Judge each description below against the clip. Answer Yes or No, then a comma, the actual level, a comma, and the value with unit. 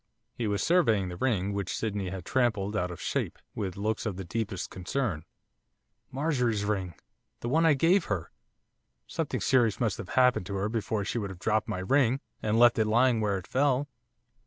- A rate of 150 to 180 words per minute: No, average, 190 wpm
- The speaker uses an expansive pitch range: No, average, 4.4 semitones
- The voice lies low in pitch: Yes, low, 110 Hz